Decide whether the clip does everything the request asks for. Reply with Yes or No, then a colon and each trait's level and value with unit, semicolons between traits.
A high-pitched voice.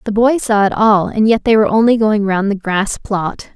Yes: high, 210 Hz